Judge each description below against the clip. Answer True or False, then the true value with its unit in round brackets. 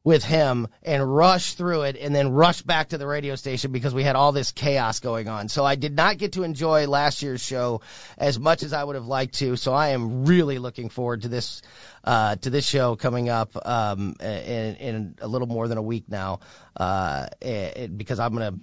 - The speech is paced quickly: True (225 wpm)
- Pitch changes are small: False (3.8 semitones)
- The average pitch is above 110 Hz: True (135 Hz)